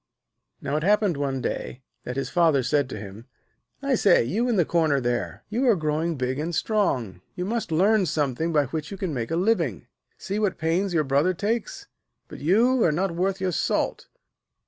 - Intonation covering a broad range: Yes, wide, 6.0 semitones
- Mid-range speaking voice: Yes, medium, 165 Hz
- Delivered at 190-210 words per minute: Yes, average, 195 wpm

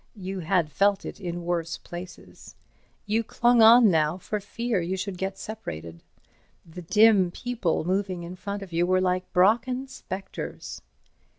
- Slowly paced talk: No, average, 155 wpm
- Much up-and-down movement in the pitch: No, average, 3.3 semitones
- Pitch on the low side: No, high, 190 Hz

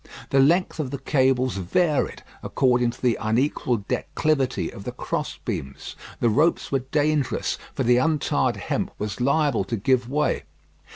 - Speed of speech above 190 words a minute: No, average, 155 wpm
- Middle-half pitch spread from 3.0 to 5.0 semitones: Yes, average, 3.6 semitones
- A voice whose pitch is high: No, low, 130 Hz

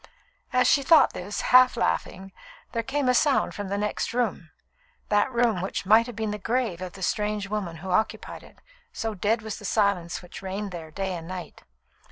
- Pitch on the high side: Yes, high, 205 Hz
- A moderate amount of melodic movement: Yes, average, 3.7 semitones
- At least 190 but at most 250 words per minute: Yes, average, 200 wpm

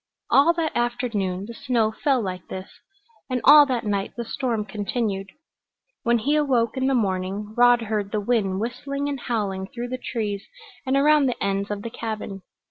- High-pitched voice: Yes, high, 230 Hz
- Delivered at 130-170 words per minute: No, average, 180 wpm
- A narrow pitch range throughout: No, average, 4.1 semitones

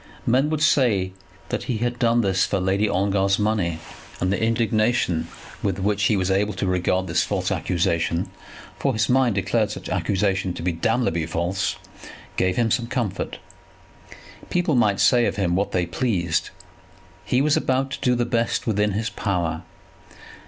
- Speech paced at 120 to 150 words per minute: No, average, 165 wpm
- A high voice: No, low, 100 Hz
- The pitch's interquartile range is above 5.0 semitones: No, average, 4.4 semitones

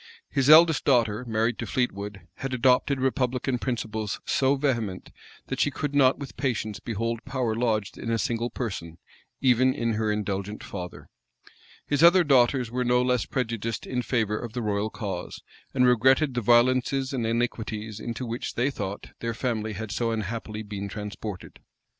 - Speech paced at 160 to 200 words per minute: Yes, average, 165 wpm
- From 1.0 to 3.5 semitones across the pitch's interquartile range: Yes, average, 3.1 semitones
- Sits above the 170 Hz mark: No, low, 120 Hz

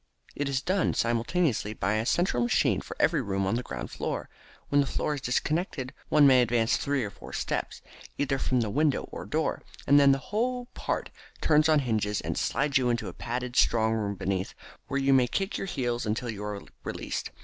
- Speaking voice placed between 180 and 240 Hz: No, low, 125 Hz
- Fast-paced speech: Yes, fast, 210 wpm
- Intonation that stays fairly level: No, average, 4.4 semitones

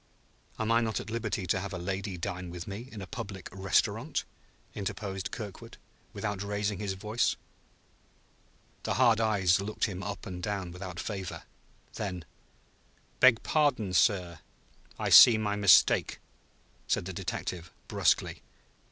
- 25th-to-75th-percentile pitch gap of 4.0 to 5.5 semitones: No, average, 2.7 semitones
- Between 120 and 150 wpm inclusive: Yes, average, 140 wpm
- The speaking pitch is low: Yes, low, 100 Hz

